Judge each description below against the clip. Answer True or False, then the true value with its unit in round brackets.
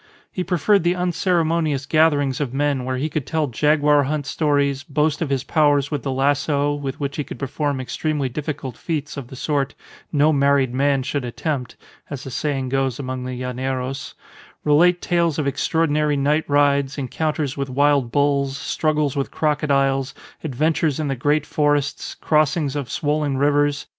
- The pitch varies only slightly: True (2.0 semitones)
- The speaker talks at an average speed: True (165 wpm)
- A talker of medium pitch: True (145 Hz)